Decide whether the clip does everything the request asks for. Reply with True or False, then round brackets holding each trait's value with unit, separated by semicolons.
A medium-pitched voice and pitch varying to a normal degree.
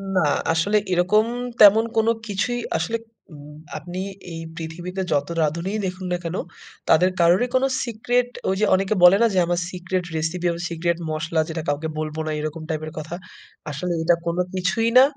True (175 Hz; 3.4 semitones)